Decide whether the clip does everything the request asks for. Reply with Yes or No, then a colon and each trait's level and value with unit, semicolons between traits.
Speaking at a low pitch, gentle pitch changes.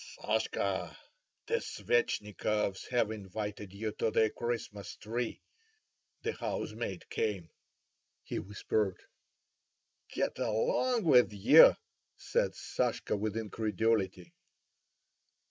Yes: low, 110 Hz; narrow, 2.2 semitones